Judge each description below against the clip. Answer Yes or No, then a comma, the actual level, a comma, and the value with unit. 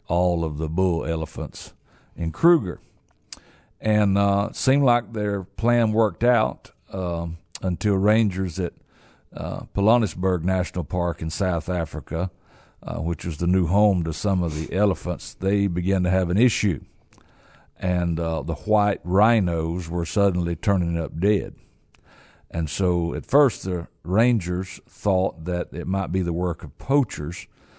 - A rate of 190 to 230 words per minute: No, average, 150 wpm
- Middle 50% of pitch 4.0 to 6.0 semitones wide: No, average, 3.2 semitones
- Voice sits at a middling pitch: No, very low, 90 Hz